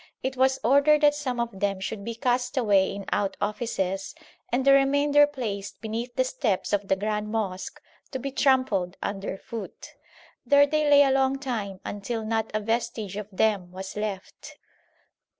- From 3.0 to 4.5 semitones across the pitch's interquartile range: No, average, 4.9 semitones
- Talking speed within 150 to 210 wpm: Yes, average, 170 wpm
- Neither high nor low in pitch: No, high, 225 Hz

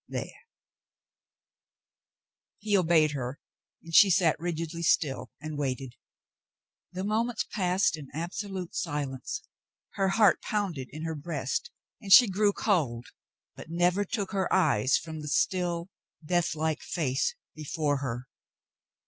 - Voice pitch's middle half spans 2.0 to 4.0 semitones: No, average, 4.8 semitones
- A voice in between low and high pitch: Yes, medium, 165 Hz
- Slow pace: Yes, slow, 125 wpm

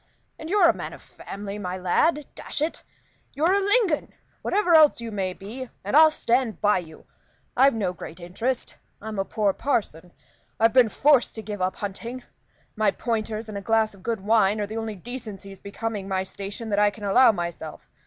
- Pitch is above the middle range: Yes, high, 215 Hz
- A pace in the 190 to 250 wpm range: Yes, average, 195 wpm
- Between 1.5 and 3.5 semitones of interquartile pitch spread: No, average, 4.5 semitones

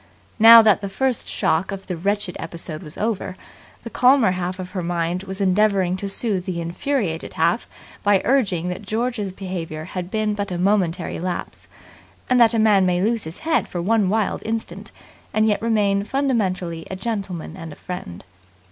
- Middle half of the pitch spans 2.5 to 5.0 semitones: Yes, average, 3.5 semitones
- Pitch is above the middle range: Yes, high, 195 Hz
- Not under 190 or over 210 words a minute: No, average, 180 wpm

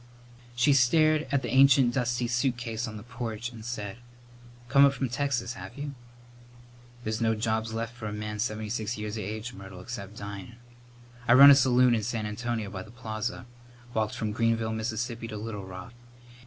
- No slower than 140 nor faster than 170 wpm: No, average, 180 wpm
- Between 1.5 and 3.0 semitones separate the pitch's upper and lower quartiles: Yes, narrow, 2.4 semitones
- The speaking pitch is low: Yes, low, 115 Hz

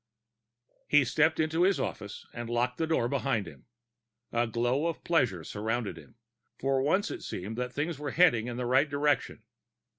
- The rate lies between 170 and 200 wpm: Yes, average, 175 wpm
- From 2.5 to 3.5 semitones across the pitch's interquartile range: No, average, 4.5 semitones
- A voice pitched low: Yes, low, 130 Hz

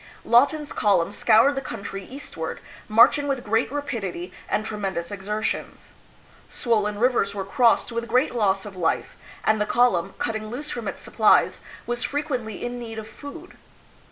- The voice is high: Yes, high, 225 Hz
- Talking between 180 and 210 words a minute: No, average, 155 wpm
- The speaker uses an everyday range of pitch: Yes, average, 3.6 semitones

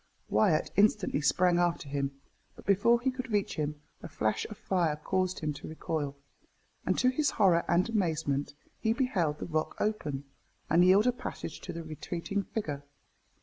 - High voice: No, medium, 175 Hz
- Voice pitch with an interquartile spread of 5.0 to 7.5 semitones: Yes, wide, 5.6 semitones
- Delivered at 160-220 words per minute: Yes, average, 170 wpm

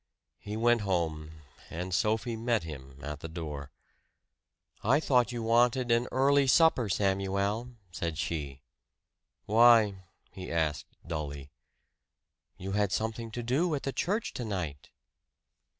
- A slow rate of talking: Yes, slow, 125 wpm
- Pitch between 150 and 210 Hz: No, low, 105 Hz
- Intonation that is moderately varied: No, wide, 6.6 semitones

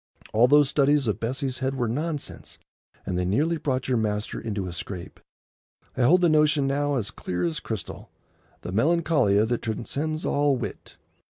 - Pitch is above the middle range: No, low, 130 Hz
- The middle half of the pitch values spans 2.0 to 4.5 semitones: No, wide, 5.4 semitones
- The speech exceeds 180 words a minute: No, average, 165 wpm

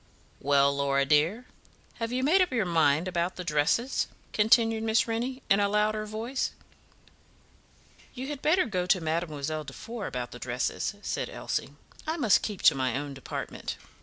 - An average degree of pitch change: No, wide, 7.9 semitones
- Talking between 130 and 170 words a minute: Yes, average, 165 wpm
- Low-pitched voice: No, high, 195 Hz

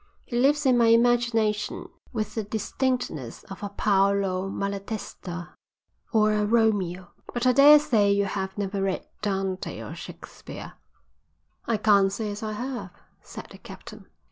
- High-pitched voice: Yes, high, 210 Hz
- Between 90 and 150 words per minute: Yes, average, 140 wpm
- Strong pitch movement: No, average, 3.2 semitones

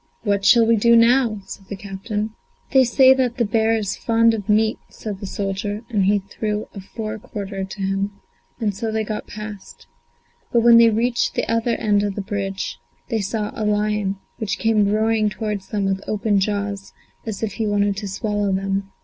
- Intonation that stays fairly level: Yes, narrow, 2.0 semitones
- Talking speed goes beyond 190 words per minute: Yes, average, 200 wpm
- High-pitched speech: Yes, high, 210 Hz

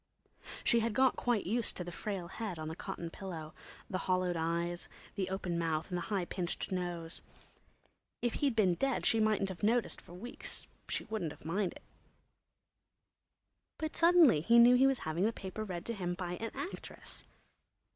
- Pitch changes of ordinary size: Yes, average, 4.8 semitones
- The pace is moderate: Yes, average, 175 wpm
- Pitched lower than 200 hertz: Yes, high, 190 Hz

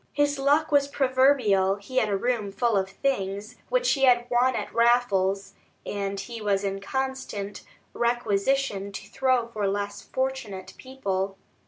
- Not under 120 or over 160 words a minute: Yes, average, 150 wpm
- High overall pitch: Yes, high, 230 Hz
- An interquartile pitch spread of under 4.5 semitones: No, average, 5.0 semitones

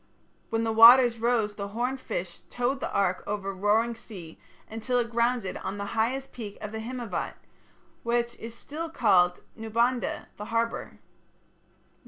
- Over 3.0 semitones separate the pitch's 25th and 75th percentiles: No, average, 2.7 semitones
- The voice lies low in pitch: No, high, 230 Hz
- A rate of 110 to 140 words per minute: No, average, 155 wpm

